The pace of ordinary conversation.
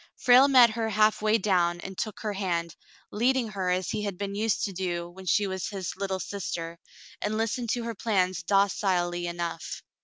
Yes: average, 185 wpm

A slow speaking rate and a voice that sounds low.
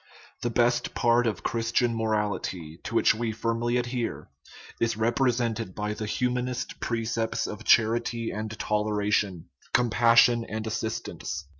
Yes: slow, 125 wpm; low, 115 Hz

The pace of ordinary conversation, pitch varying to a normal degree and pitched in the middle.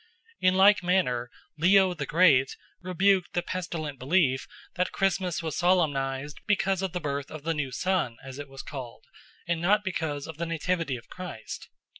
Yes: average, 170 wpm; average, 4.8 semitones; medium, 165 Hz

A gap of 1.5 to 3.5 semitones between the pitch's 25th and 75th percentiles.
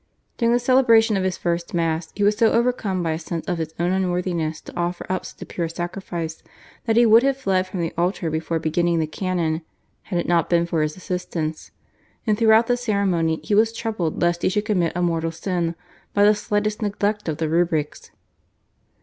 No: average, 4.0 semitones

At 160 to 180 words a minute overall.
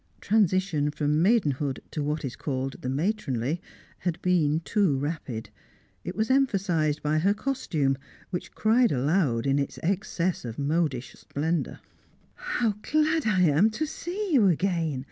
No: average, 145 wpm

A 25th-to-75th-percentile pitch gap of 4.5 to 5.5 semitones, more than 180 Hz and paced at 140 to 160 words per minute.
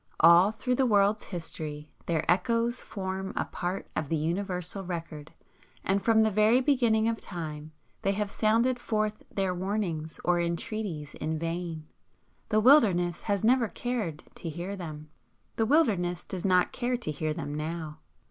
Yes: average, 4.8 semitones; high, 190 Hz; average, 155 wpm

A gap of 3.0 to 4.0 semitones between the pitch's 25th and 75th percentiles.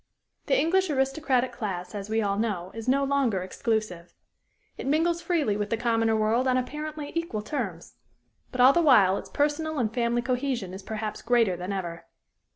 No: average, 5.3 semitones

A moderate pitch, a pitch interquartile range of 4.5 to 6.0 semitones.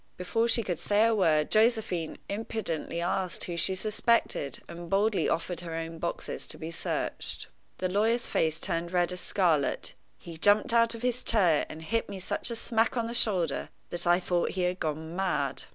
Yes: medium, 180 Hz; average, 4.8 semitones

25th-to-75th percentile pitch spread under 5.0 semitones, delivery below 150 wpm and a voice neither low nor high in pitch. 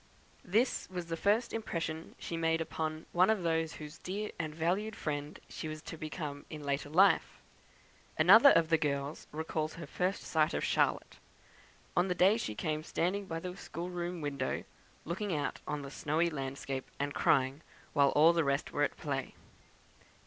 No: average, 3.3 semitones; average, 170 wpm; medium, 160 Hz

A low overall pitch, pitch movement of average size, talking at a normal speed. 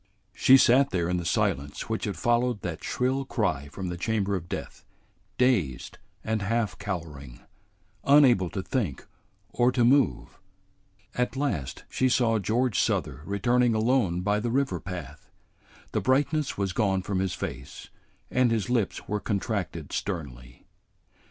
No: low, 105 Hz; wide, 5.8 semitones; average, 145 wpm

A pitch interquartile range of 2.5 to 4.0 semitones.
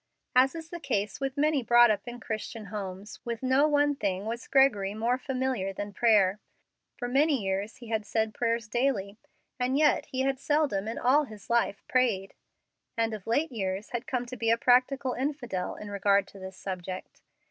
No: average, 4.4 semitones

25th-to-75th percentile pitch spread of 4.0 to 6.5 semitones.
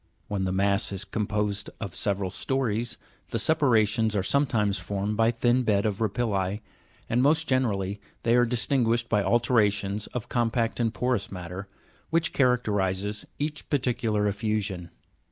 No: average, 3.4 semitones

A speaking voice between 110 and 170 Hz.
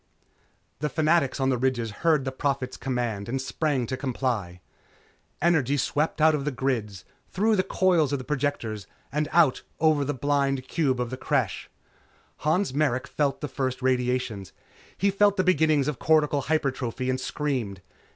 Yes: low, 135 Hz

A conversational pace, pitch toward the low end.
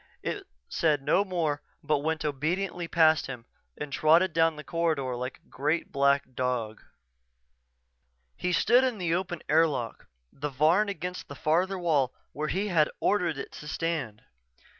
No: average, 155 wpm; medium, 155 Hz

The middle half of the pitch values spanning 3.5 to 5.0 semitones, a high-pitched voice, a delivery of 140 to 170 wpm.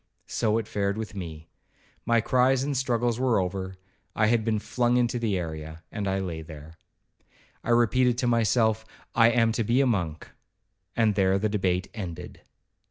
No: average, 4.1 semitones; low, 110 Hz; average, 165 wpm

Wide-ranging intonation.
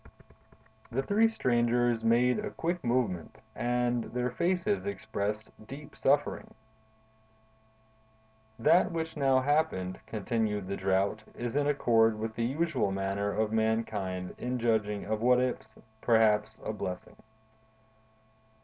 No: average, 3.6 semitones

